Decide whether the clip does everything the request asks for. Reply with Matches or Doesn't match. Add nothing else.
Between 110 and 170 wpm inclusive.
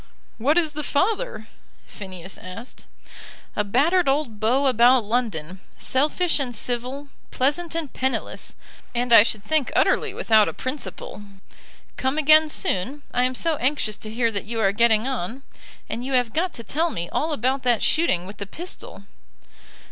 Matches